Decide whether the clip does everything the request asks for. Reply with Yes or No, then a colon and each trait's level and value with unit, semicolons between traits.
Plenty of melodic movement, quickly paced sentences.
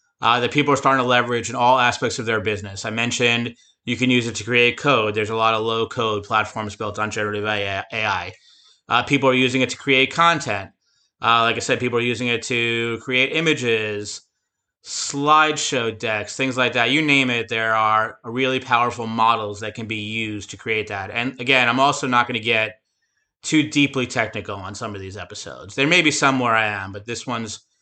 No: average, 3.1 semitones; fast, 210 wpm